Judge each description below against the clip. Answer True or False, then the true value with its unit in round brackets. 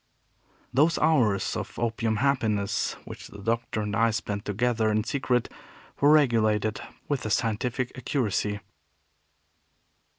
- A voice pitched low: True (115 Hz)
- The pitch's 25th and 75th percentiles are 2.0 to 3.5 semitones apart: True (3.2 semitones)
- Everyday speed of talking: False (120 wpm)